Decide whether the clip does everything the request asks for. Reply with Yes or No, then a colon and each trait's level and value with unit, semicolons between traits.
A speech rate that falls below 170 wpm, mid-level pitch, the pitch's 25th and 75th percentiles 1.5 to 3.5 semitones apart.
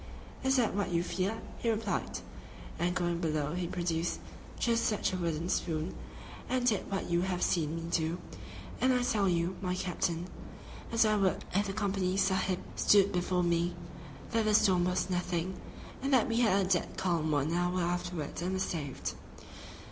No: average, 180 wpm; medium, 180 Hz; average, 2.7 semitones